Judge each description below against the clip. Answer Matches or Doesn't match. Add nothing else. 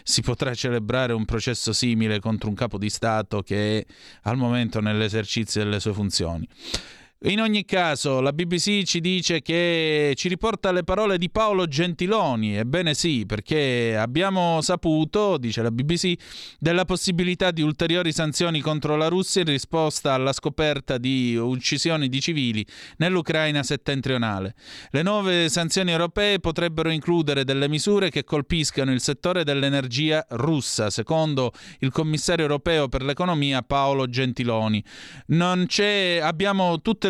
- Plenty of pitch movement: Matches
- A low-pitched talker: Doesn't match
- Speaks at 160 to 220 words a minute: Doesn't match